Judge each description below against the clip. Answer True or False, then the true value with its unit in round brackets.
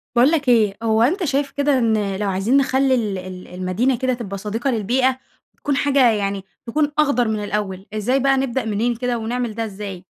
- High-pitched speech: True (230 Hz)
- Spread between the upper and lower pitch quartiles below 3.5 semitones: False (4.4 semitones)